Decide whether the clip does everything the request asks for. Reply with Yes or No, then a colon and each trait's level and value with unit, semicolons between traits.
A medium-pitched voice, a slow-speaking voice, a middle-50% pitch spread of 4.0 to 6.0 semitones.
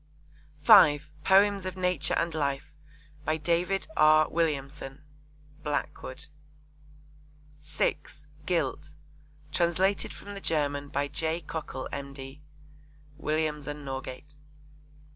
No: medium, 150 Hz; slow, 95 wpm; average, 2.8 semitones